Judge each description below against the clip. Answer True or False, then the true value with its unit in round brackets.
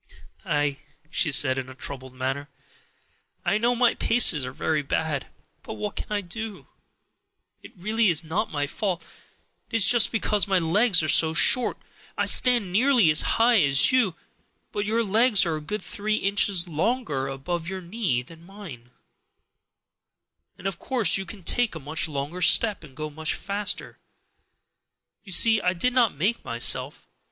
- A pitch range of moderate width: False (6.2 semitones)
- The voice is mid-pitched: True (180 Hz)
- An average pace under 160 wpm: False (165 wpm)